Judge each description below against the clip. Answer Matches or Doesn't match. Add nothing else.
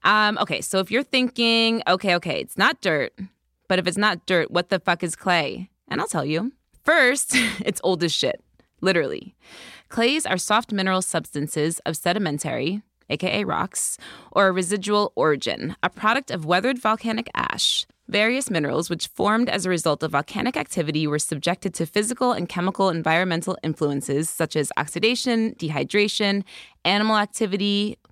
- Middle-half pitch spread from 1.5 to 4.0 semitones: Doesn't match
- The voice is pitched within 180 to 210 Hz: Matches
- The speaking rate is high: Doesn't match